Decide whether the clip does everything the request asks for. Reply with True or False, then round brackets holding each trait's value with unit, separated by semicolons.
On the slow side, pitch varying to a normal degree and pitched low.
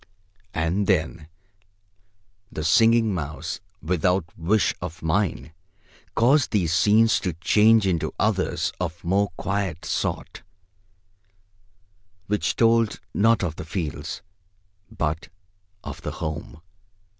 True (105 wpm; 4.6 semitones; 90 Hz)